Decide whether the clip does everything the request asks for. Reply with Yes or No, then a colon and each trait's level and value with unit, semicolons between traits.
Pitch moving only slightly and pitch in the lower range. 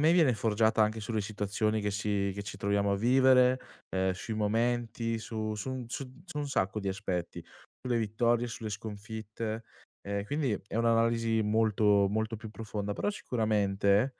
Yes: narrow, 2.3 semitones; low, 110 Hz